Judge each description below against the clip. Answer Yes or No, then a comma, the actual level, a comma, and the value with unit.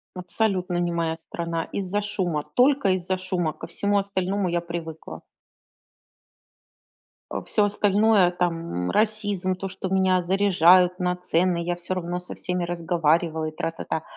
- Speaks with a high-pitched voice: No, medium, 180 Hz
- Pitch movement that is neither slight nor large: No, narrow, 2.2 semitones